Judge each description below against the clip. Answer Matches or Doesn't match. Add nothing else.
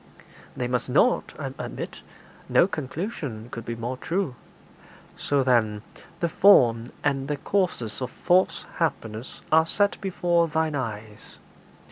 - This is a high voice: Doesn't match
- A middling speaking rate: Doesn't match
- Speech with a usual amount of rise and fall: Doesn't match